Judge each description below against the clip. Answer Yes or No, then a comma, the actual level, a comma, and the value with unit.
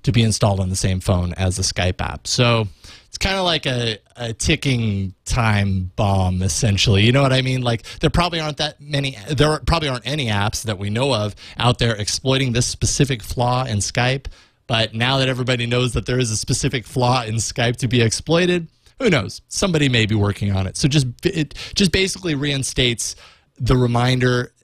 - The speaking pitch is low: Yes, low, 120 Hz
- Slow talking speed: No, average, 200 wpm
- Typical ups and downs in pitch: Yes, average, 4.8 semitones